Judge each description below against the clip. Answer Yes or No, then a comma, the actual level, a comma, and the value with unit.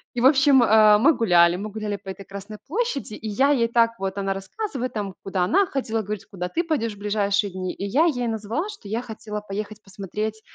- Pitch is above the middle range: Yes, high, 215 Hz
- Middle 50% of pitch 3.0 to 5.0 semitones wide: Yes, average, 3.9 semitones